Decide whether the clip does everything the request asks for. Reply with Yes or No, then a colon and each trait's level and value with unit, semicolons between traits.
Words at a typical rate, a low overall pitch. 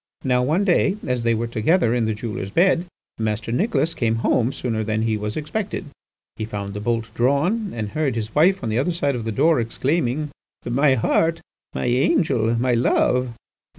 Yes: average, 185 wpm; low, 125 Hz